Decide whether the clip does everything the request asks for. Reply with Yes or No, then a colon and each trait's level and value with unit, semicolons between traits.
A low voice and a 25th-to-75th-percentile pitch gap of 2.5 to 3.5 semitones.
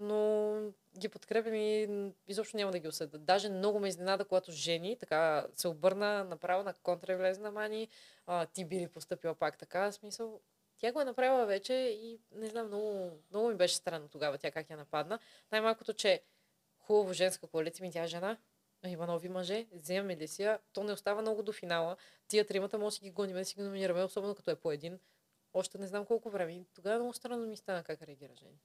No: high, 195 Hz; average, 3.2 semitones